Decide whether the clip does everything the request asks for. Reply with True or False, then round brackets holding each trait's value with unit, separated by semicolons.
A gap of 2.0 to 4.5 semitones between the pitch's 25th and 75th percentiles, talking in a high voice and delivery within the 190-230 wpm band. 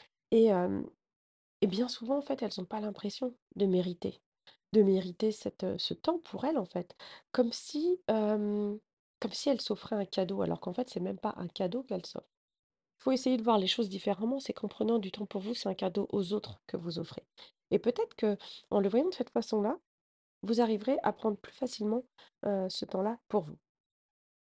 True (3.8 semitones; 215 Hz; 205 wpm)